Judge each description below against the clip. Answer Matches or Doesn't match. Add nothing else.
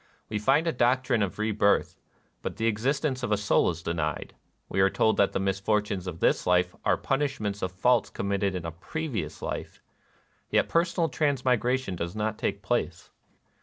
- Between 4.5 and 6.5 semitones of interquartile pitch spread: Matches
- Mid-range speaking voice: Doesn't match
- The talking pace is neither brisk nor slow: Matches